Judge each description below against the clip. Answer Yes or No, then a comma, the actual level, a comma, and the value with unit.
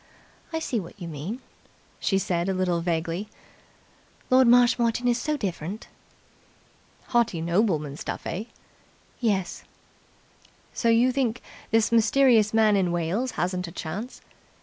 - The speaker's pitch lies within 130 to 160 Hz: No, high, 210 Hz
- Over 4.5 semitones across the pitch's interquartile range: Yes, wide, 5.4 semitones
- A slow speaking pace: Yes, slow, 125 wpm